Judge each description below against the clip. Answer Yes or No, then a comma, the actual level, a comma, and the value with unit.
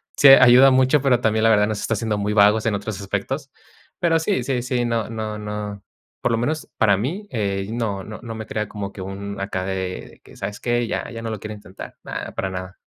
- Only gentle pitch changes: No, average, 3.0 semitones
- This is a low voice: Yes, low, 110 Hz